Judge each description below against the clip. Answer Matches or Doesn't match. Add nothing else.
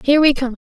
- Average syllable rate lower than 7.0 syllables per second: Doesn't match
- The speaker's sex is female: Matches